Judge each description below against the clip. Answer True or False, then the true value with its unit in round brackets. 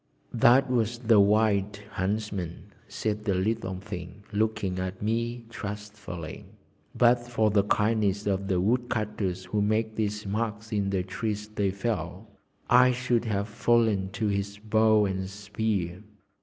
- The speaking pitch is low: True (105 Hz)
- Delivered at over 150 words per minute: False (140 wpm)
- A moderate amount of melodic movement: False (2.2 semitones)